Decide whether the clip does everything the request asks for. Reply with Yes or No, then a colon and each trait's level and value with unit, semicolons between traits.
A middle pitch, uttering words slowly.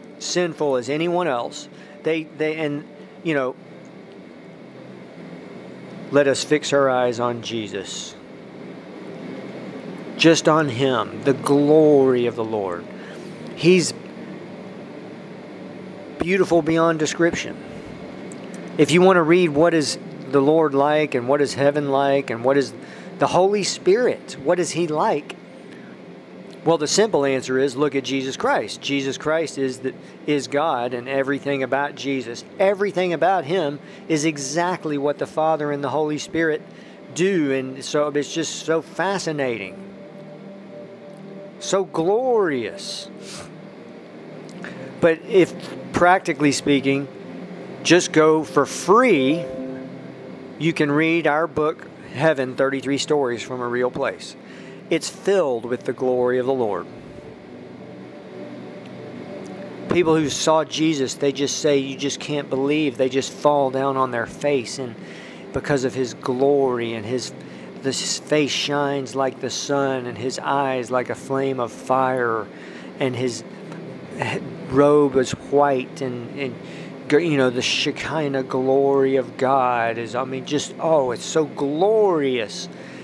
Yes: medium, 145 Hz; slow, 130 wpm